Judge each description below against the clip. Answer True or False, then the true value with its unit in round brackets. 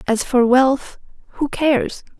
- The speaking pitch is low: False (260 Hz)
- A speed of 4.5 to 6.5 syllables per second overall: False (4.0 syllables/s)